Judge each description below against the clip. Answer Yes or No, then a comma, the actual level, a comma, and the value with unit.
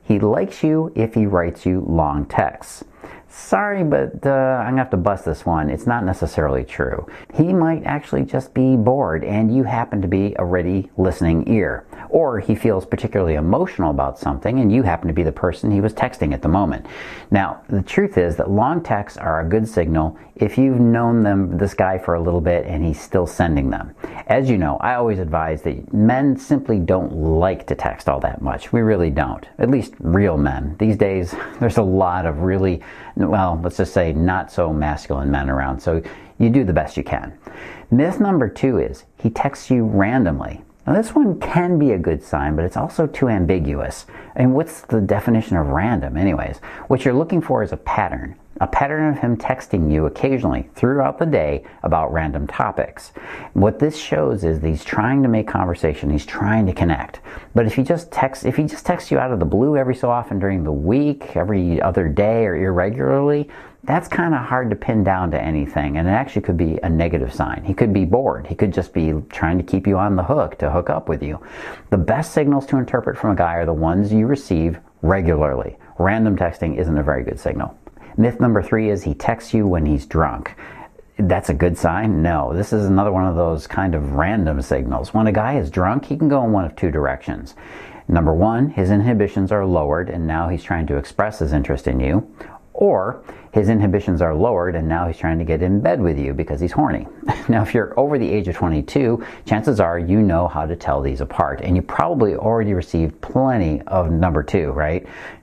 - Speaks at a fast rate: Yes, fast, 215 wpm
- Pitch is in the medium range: No, very low, 95 Hz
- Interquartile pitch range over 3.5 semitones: Yes, wide, 5.6 semitones